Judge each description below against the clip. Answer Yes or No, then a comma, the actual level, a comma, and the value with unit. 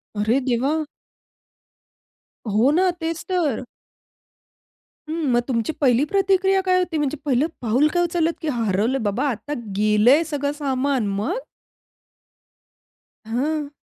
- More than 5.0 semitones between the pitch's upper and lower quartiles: Yes, wide, 5.4 semitones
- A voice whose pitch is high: Yes, very high, 285 Hz